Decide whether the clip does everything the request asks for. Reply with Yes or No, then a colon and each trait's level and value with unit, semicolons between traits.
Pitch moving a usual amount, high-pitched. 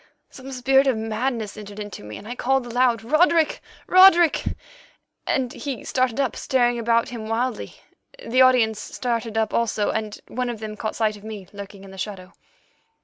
Yes: average, 3.2 semitones; high, 230 Hz